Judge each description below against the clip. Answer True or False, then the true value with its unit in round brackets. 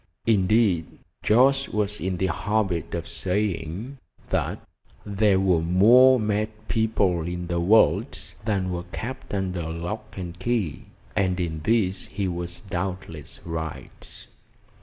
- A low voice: True (95 Hz)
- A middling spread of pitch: True (3.7 semitones)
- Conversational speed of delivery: False (125 wpm)